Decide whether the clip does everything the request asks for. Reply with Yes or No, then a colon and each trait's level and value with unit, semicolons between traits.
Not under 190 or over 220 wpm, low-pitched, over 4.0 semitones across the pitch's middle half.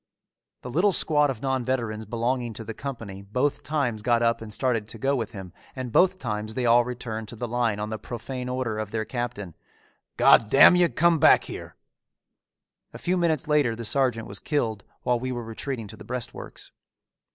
No: average, 195 wpm; low, 120 Hz; average, 3.2 semitones